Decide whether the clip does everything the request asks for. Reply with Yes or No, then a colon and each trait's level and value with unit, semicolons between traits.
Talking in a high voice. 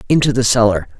No: low, 120 Hz